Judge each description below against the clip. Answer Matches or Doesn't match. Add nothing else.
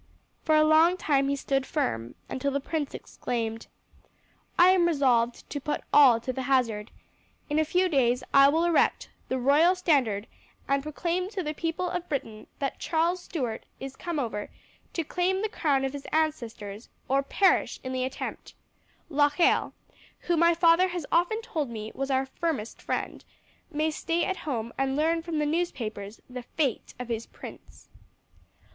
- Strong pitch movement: Doesn't match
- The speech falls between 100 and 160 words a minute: Doesn't match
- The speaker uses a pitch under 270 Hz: Doesn't match